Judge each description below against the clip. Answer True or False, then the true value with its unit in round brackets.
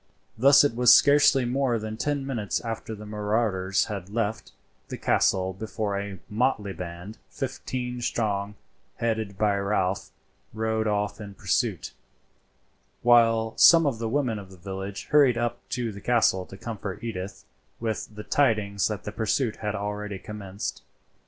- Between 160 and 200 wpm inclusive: False (150 wpm)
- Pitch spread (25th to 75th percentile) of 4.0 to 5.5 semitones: False (3.0 semitones)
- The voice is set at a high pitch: False (110 Hz)